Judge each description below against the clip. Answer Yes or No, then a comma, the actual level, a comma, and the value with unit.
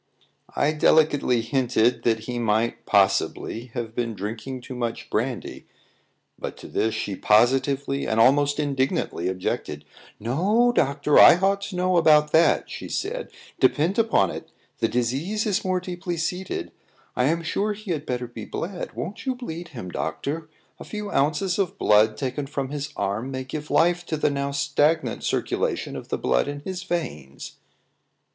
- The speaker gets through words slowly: No, average, 165 wpm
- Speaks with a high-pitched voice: No, medium, 140 Hz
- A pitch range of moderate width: No, wide, 6.3 semitones